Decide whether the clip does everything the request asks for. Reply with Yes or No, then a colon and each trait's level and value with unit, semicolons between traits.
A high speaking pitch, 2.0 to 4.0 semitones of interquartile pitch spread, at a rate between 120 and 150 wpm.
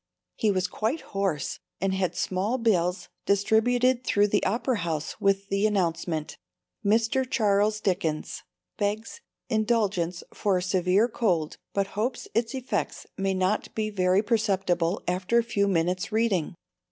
Yes: high, 200 Hz; average, 3.3 semitones; average, 140 wpm